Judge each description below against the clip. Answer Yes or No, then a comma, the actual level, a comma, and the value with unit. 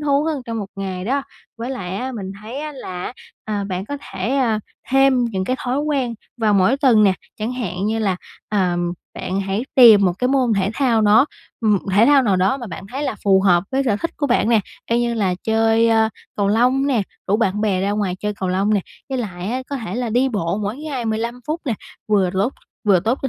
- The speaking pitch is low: No, high, 220 Hz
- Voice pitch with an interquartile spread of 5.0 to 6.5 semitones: No, average, 4.6 semitones